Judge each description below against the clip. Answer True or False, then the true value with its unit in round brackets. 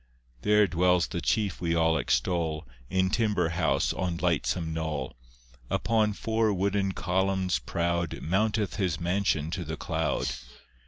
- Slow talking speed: True (130 wpm)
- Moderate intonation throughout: True (3.2 semitones)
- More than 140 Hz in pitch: False (90 Hz)